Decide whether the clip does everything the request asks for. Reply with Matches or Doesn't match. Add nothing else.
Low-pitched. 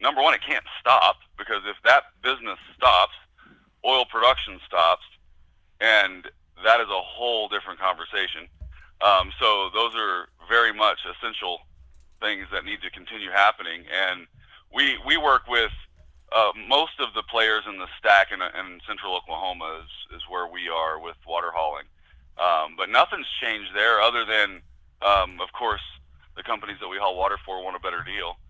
Matches